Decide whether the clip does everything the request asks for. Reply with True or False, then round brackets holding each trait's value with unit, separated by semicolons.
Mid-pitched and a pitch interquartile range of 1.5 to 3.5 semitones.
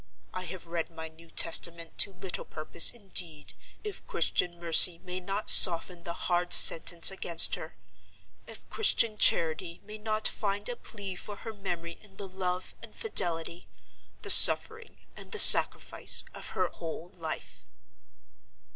True (180 Hz; 3.1 semitones)